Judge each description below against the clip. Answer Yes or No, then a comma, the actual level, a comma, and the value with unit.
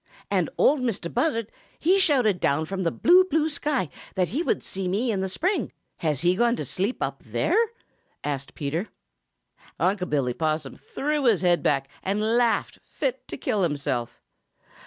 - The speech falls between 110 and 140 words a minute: No, average, 170 wpm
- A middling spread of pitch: No, wide, 8.5 semitones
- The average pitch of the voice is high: Yes, high, 195 Hz